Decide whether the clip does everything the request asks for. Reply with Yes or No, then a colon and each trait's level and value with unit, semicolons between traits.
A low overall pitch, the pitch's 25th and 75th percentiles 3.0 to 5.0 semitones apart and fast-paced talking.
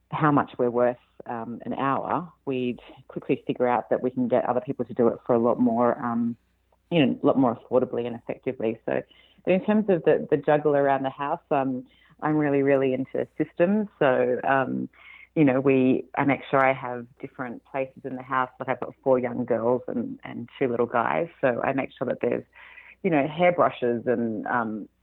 No: low, 130 Hz; narrow, 2.5 semitones; fast, 210 wpm